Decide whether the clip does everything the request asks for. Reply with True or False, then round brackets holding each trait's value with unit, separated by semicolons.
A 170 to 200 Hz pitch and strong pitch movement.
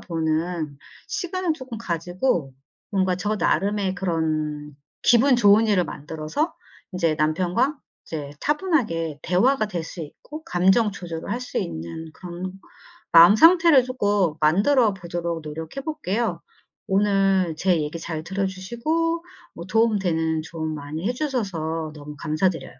True (185 Hz; 5.9 semitones)